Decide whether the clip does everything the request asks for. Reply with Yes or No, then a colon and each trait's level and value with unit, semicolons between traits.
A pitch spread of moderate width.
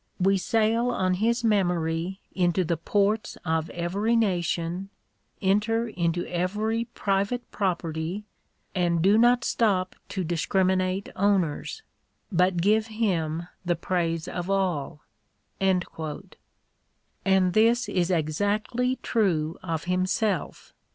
Yes: average, 3.7 semitones